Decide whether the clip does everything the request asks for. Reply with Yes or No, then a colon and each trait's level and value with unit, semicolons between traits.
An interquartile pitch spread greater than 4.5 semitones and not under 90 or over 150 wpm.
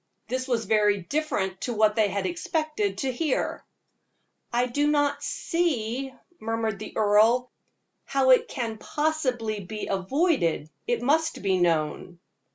Yes: wide, 5.5 semitones; slow, 135 wpm